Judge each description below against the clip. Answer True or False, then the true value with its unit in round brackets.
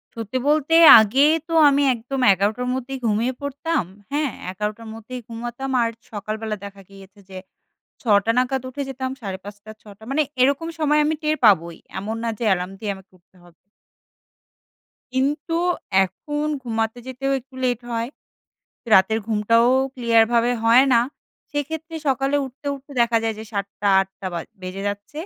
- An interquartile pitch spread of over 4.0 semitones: True (4.5 semitones)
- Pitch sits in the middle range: False (235 Hz)